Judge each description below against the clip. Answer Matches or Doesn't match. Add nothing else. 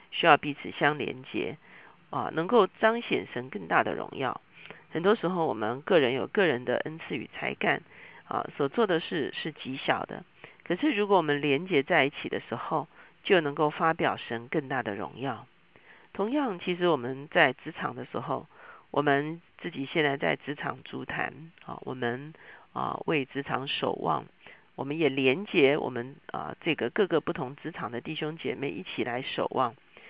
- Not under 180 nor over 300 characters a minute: Matches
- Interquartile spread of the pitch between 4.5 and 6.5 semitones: Doesn't match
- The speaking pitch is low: Doesn't match